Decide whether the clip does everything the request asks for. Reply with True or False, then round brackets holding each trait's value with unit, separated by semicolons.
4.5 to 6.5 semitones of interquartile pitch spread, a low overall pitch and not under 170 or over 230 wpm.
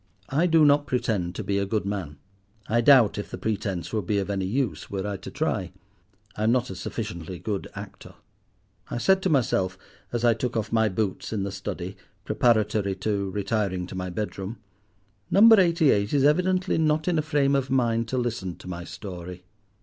True (5.5 semitones; 110 Hz; 195 wpm)